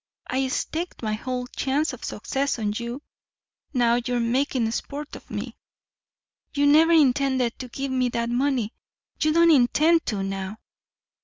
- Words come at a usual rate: Yes, average, 150 wpm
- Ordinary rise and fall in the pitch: Yes, average, 3.4 semitones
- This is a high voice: Yes, very high, 255 Hz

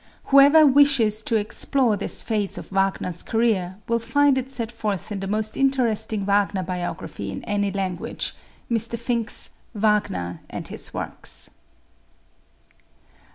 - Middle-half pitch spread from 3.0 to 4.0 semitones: Yes, average, 3.3 semitones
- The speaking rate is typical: No, slow, 130 wpm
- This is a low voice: No, high, 215 Hz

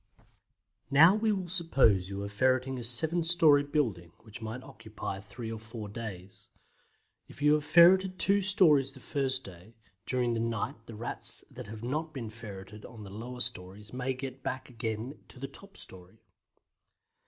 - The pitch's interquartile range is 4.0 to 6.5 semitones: Yes, average, 5.2 semitones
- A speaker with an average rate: Yes, average, 170 wpm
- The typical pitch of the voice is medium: No, low, 125 Hz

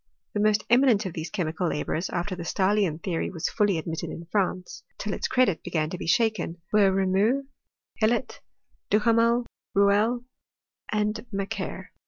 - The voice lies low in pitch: No, high, 200 Hz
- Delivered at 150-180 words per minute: Yes, average, 160 wpm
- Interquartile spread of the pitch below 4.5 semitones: Yes, average, 3.7 semitones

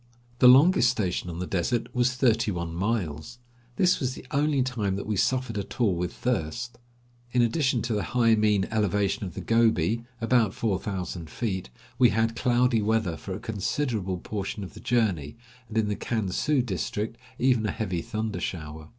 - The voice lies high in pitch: No, low, 110 Hz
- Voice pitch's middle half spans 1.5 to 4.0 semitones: No, average, 4.4 semitones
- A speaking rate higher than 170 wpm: Yes, average, 185 wpm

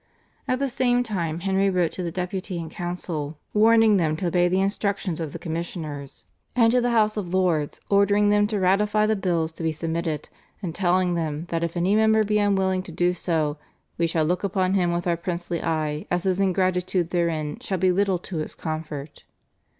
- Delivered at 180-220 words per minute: Yes, average, 200 wpm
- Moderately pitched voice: Yes, medium, 180 Hz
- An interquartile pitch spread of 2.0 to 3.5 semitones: Yes, average, 3.2 semitones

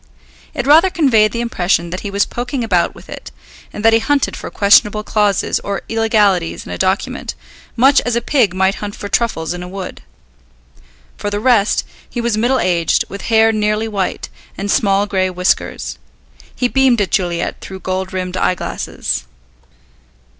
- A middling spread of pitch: Yes, average, 3.7 semitones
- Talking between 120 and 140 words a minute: No, average, 170 wpm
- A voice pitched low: No, high, 205 Hz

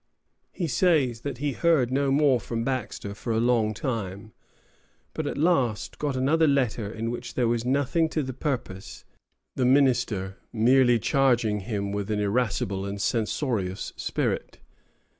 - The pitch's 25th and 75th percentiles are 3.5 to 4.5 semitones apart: Yes, average, 4.2 semitones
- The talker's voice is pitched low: Yes, low, 120 Hz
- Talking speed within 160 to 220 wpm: No, average, 150 wpm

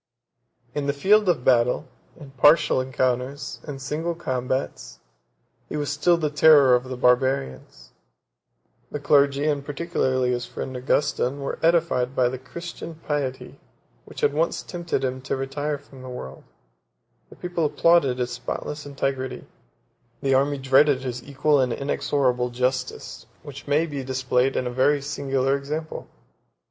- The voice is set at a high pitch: No, low, 135 Hz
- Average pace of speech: Yes, average, 145 wpm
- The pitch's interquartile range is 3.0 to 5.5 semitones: No, narrow, 2.4 semitones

